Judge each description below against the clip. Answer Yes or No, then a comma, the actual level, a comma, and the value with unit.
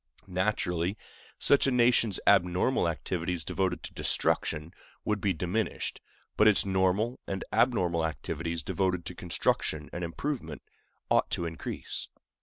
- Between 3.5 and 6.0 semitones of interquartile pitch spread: Yes, average, 4.0 semitones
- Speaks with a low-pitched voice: Yes, very low, 90 Hz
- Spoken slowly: Yes, slow, 125 wpm